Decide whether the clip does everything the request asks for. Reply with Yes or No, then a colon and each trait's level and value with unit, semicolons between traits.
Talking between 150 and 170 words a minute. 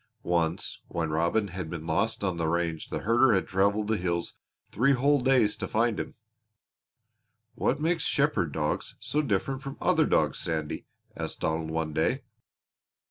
Yes: average, 160 wpm